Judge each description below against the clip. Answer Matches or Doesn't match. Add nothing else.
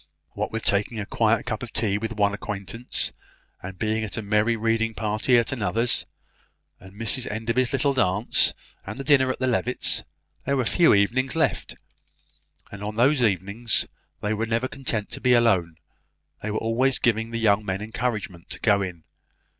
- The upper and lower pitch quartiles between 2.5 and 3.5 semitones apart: Matches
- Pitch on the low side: Matches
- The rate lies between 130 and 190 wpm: Matches